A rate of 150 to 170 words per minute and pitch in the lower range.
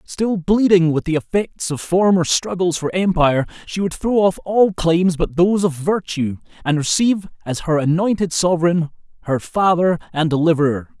No: average, 165 wpm; medium, 175 Hz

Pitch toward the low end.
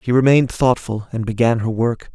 Yes: low, 120 Hz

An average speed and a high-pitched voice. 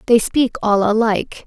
Yes: average, 165 wpm; high, 220 Hz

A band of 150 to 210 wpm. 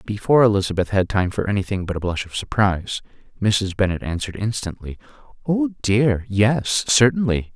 No: slow, 135 wpm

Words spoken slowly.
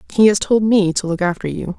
No: fast, 270 wpm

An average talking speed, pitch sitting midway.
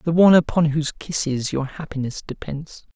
Yes: average, 165 wpm; medium, 150 Hz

